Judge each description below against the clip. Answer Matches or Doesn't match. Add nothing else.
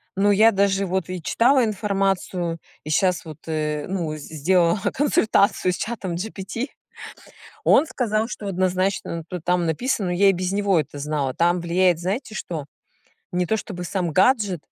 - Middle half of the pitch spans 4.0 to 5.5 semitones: Doesn't match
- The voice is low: Doesn't match